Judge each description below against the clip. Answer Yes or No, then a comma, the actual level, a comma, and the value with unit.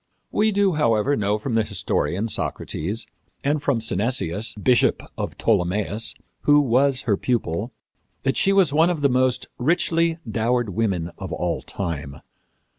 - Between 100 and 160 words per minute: Yes, average, 145 wpm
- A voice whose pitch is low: Yes, low, 115 Hz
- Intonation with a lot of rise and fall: Yes, wide, 5.8 semitones